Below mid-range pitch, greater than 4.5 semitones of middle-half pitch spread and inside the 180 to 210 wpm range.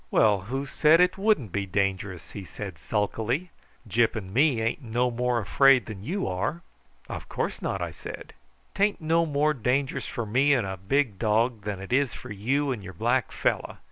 Yes: low, 120 Hz; wide, 5.5 semitones; average, 190 wpm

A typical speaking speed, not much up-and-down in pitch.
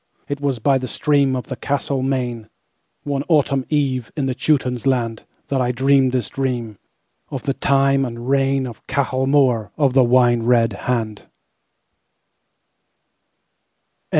No: slow, 125 wpm; narrow, 2.2 semitones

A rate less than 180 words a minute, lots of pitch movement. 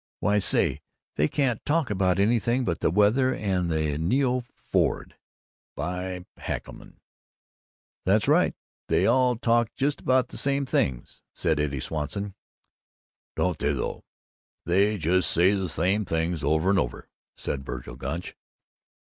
Yes: average, 140 wpm; wide, 6.8 semitones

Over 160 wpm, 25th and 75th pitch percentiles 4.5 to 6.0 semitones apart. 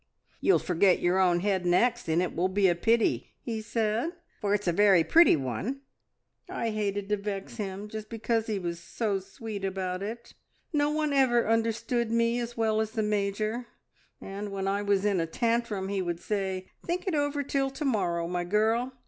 No: average, 190 wpm; average, 3.5 semitones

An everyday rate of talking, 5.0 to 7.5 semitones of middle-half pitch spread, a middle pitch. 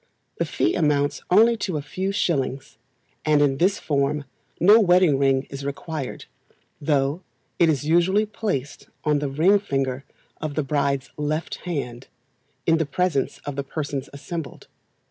No: average, 150 wpm; average, 3.9 semitones; medium, 150 Hz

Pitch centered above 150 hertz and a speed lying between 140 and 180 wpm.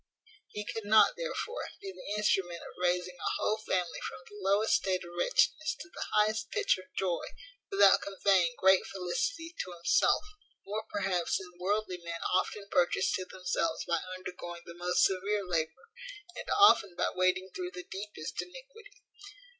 Yes: high, 190 Hz; average, 160 wpm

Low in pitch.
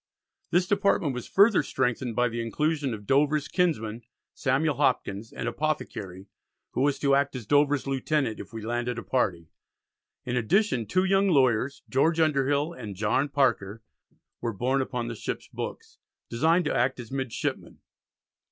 Yes: low, 130 Hz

